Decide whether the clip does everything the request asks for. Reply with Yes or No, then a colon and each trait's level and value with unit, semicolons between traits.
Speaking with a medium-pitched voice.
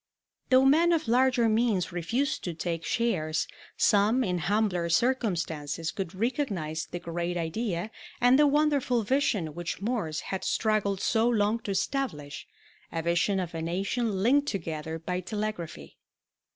No: high, 200 Hz